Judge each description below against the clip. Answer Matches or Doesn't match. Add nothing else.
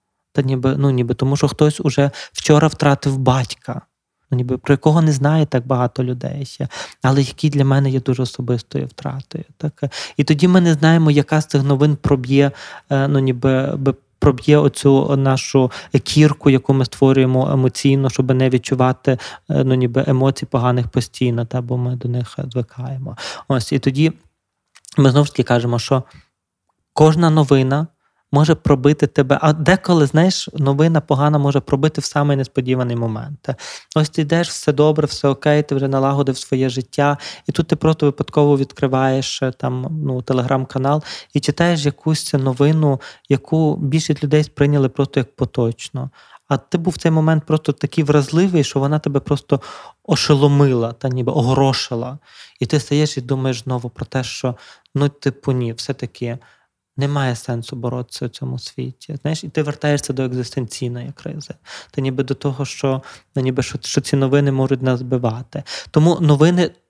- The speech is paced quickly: Matches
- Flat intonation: Matches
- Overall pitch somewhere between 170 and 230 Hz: Doesn't match